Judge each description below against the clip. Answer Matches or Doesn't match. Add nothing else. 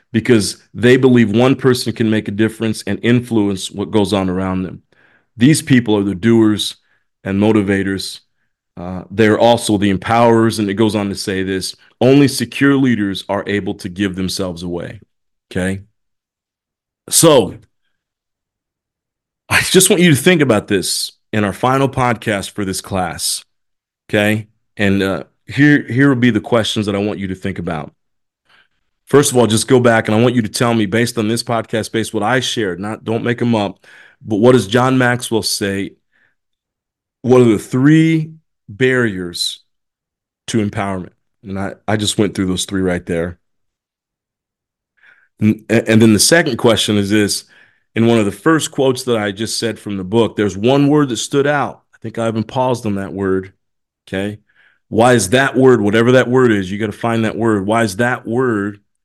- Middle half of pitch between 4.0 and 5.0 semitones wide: Doesn't match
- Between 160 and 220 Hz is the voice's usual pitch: Doesn't match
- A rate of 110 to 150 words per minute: Doesn't match